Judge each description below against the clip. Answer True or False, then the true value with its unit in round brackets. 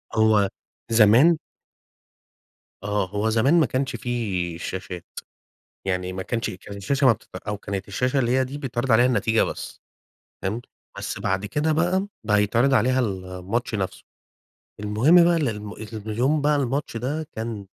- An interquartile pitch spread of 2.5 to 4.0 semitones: False (4.6 semitones)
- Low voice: True (115 Hz)